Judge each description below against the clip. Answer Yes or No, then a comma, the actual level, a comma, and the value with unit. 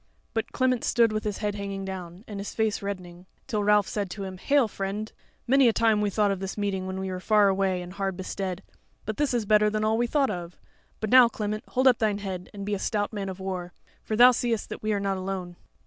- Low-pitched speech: No, high, 205 Hz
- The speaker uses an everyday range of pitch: No, narrow, 2.3 semitones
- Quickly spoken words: Yes, fast, 250 wpm